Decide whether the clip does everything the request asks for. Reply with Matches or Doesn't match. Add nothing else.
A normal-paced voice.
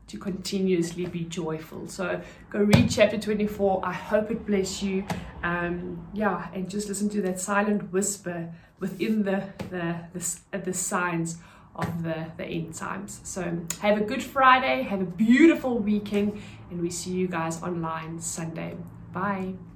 Matches